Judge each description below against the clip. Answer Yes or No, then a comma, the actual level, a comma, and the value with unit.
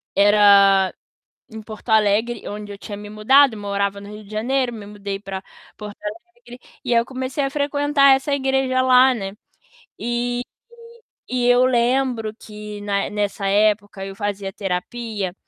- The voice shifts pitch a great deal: No, average, 3.8 semitones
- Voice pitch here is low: No, high, 215 Hz